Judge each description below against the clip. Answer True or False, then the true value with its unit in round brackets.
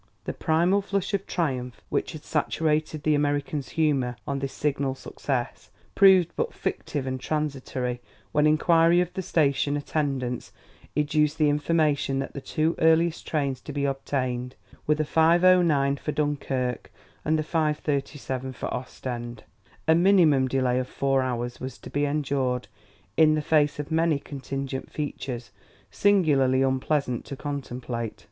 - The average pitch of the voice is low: False (145 Hz)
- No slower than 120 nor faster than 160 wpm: True (145 wpm)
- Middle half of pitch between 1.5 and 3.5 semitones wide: True (3.1 semitones)